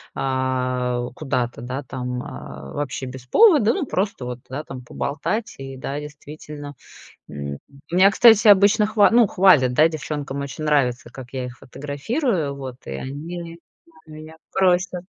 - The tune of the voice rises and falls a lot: Yes, wide, 5.7 semitones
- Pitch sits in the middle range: Yes, medium, 145 Hz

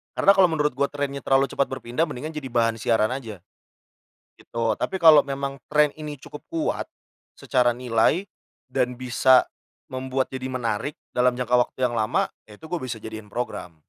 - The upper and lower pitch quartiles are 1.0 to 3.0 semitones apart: No, average, 3.5 semitones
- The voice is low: Yes, low, 130 Hz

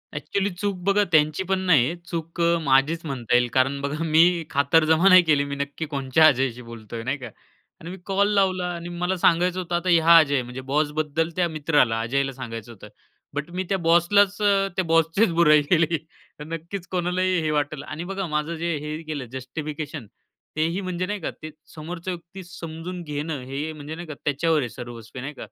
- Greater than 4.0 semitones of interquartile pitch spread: No, average, 3.7 semitones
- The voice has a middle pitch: Yes, medium, 160 Hz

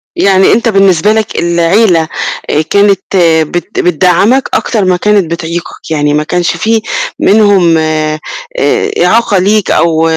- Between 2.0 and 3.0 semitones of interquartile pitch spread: No, average, 4.0 semitones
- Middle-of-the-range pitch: Yes, medium, 180 Hz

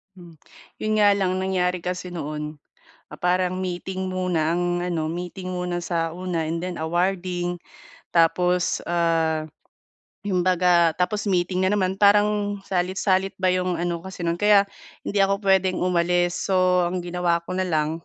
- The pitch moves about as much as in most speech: No, narrow, 1.4 semitones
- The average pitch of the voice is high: No, medium, 180 Hz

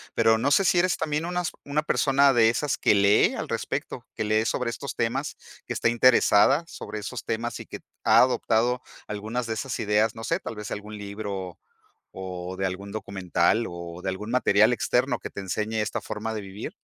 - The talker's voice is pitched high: No, low, 110 Hz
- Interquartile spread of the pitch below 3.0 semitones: No, average, 3.7 semitones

